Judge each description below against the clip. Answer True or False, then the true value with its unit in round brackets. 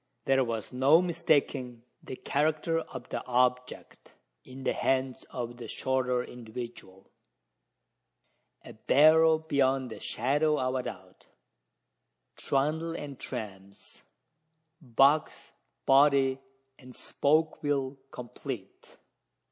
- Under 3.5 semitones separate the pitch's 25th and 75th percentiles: True (3.0 semitones)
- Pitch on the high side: False (130 Hz)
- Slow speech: True (100 wpm)